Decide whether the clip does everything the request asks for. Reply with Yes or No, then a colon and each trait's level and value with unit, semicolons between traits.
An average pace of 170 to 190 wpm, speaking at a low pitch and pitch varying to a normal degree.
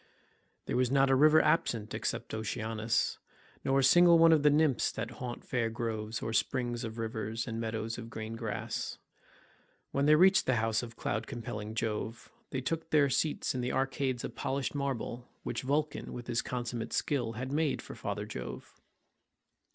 Yes: average, 175 wpm; low, 120 Hz; average, 3.6 semitones